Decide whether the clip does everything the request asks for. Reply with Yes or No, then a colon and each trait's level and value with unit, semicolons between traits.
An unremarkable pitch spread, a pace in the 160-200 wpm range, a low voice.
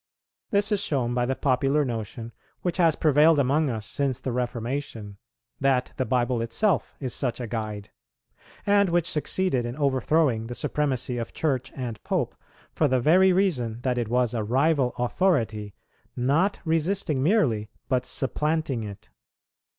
No: average, 4.7 semitones; average, 150 wpm; low, 130 Hz